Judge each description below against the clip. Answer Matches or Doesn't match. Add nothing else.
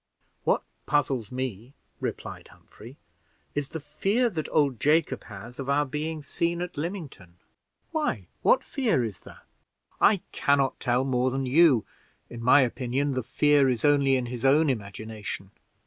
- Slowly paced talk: Doesn't match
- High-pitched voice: Doesn't match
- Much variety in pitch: Doesn't match